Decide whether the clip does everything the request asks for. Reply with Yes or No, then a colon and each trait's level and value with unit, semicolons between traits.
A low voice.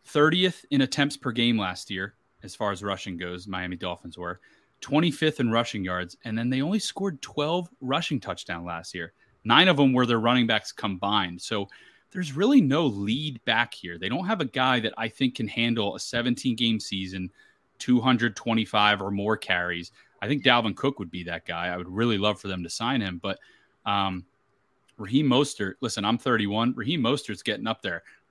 Yes: low, 115 Hz